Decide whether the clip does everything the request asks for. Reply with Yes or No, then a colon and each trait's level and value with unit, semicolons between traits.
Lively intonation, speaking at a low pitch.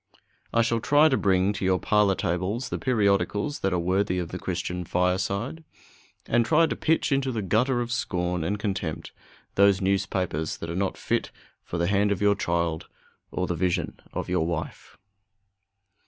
No: average, 3.7 semitones; very low, 95 Hz